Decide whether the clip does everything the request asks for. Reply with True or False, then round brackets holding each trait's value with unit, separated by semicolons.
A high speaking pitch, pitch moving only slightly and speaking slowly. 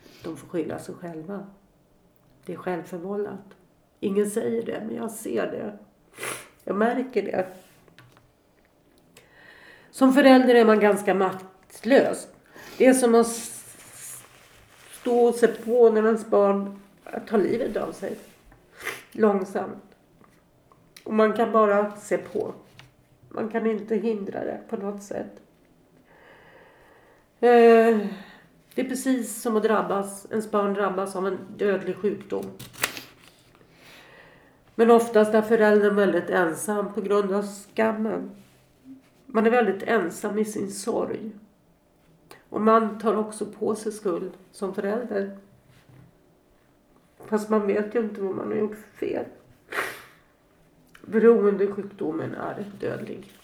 True (210 Hz; 2.3 semitones; 120 wpm)